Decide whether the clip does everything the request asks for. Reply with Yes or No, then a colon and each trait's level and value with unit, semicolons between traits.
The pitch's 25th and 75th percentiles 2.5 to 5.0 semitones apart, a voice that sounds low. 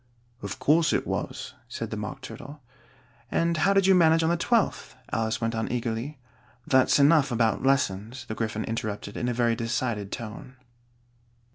No: wide, 5.4 semitones; low, 120 Hz